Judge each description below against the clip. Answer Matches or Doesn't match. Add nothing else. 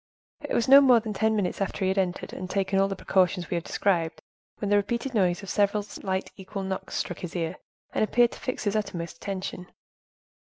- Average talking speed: Doesn't match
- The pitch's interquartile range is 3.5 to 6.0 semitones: Doesn't match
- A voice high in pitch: Matches